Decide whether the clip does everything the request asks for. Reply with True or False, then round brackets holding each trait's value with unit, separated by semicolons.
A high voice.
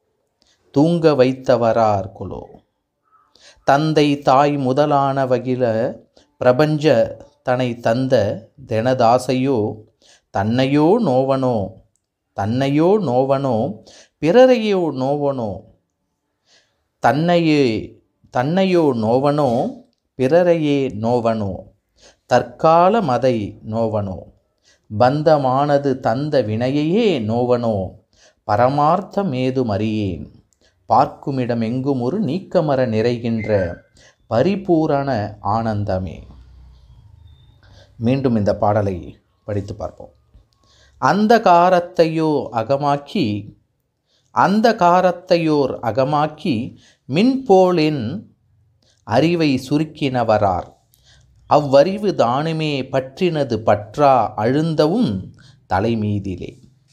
False (130 Hz)